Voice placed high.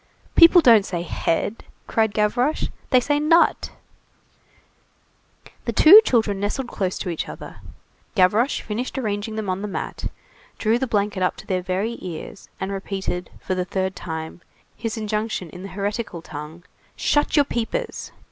Yes: high, 205 Hz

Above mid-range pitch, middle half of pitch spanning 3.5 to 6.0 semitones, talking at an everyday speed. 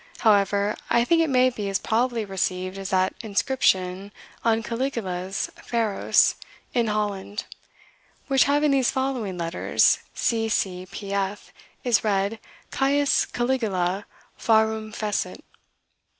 No: high, 215 Hz; average, 3.9 semitones; slow, 120 wpm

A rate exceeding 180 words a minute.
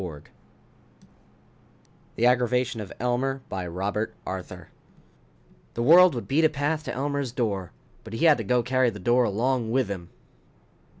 No: average, 155 wpm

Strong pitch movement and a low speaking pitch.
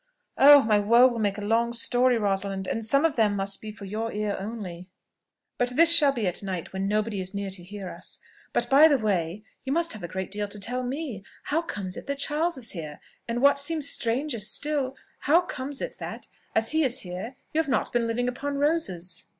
No: wide, 5.8 semitones; high, 230 Hz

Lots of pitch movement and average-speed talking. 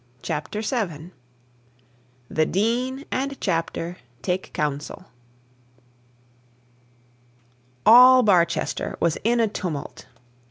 No: wide, 6.5 semitones; slow, 80 wpm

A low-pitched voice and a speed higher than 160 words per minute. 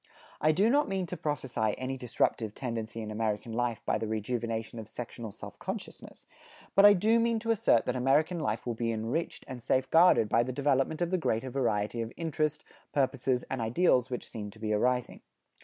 Yes: low, 125 Hz; average, 195 wpm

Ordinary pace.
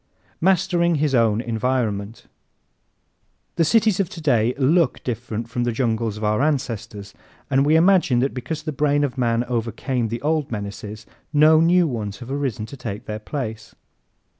Yes: average, 165 wpm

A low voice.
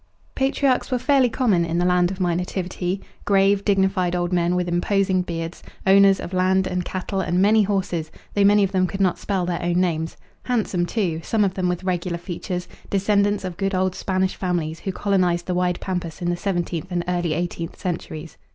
No: medium, 185 Hz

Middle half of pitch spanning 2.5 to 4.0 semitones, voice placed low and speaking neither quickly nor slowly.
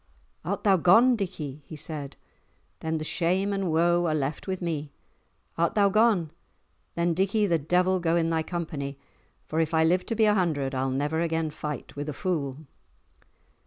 No: average, 3.4 semitones; medium, 165 Hz; average, 180 wpm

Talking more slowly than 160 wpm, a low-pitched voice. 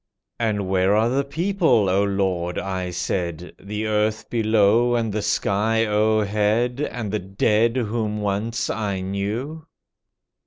Yes: average, 140 wpm; low, 105 Hz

